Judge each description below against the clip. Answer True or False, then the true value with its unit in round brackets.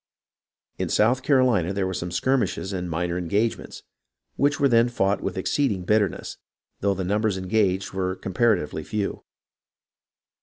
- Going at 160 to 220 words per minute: False (150 wpm)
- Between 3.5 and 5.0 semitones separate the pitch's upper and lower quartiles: True (4.0 semitones)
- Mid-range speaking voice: False (100 Hz)